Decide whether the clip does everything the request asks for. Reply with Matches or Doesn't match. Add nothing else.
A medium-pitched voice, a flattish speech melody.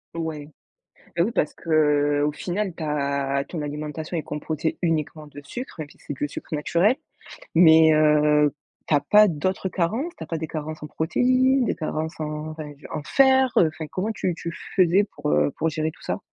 Doesn't match